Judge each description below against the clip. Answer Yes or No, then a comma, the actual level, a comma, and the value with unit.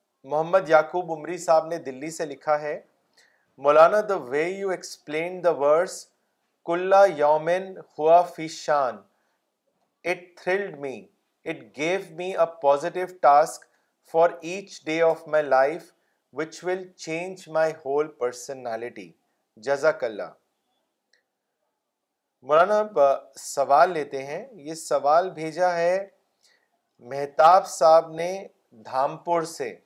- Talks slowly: Yes, slow, 80 wpm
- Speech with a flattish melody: No, average, 3.1 semitones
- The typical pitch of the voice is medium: Yes, medium, 165 Hz